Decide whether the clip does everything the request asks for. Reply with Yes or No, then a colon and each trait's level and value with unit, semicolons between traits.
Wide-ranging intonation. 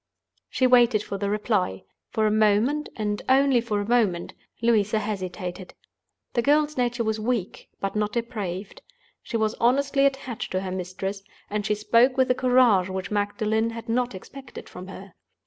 No: average, 3.7 semitones